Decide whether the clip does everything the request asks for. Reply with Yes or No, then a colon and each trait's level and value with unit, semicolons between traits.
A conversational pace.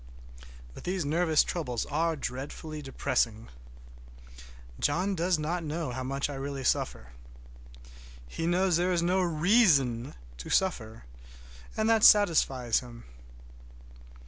No: slow, 120 wpm